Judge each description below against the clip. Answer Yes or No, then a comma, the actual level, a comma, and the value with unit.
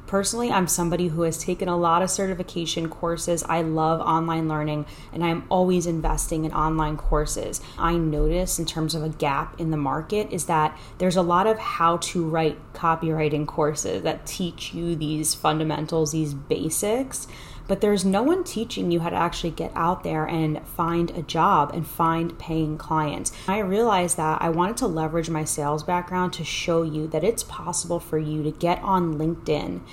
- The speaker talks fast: No, average, 185 wpm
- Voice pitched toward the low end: No, medium, 165 Hz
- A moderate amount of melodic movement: No, narrow, 2.2 semitones